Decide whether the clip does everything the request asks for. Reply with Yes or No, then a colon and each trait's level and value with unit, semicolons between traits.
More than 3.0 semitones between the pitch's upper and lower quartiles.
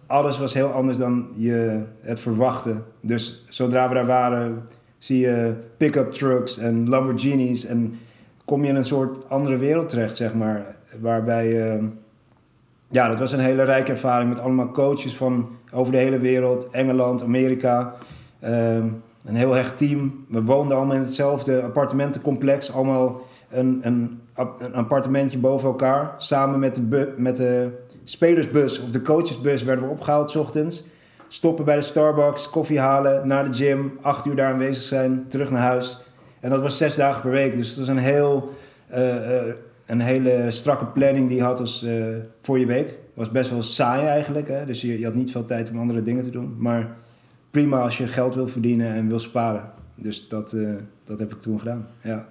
No: narrow, 2.5 semitones